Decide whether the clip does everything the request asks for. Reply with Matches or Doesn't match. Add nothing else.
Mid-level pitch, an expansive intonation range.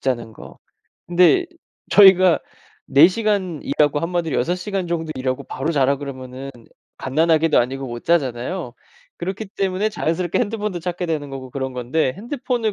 Matches